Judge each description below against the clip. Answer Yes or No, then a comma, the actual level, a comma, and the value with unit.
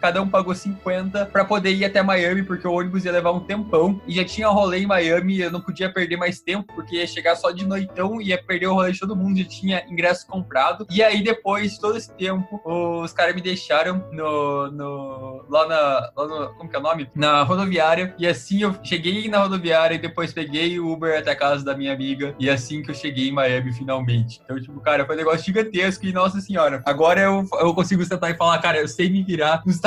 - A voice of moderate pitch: Yes, medium, 175 Hz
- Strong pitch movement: No, average, 3.6 semitones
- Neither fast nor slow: No, fast, 235 wpm